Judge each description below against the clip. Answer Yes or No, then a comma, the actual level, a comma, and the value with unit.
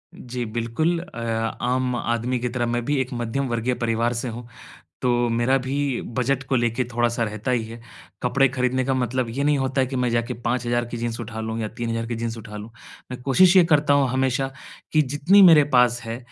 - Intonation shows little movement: Yes, narrow, 2.1 semitones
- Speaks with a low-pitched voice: Yes, low, 125 Hz